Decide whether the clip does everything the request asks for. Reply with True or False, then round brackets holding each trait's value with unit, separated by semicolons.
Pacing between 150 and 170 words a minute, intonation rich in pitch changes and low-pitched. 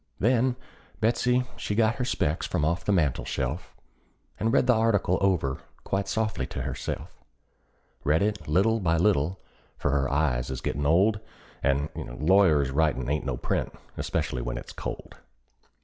True (160 wpm; 6.9 semitones; 85 Hz)